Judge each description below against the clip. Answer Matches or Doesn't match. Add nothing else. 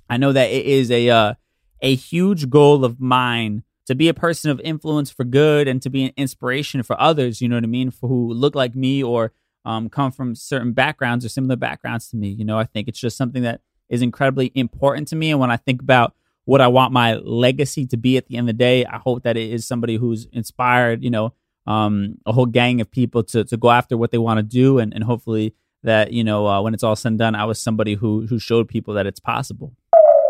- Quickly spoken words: Matches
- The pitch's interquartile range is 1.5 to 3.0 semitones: Matches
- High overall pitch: Doesn't match